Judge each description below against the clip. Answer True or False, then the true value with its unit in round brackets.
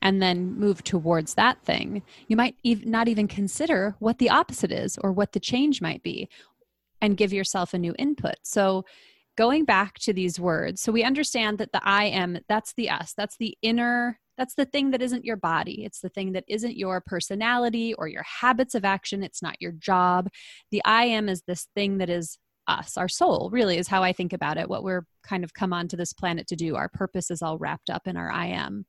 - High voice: True (200 Hz)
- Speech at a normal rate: False (220 wpm)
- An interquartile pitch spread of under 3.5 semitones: False (4.2 semitones)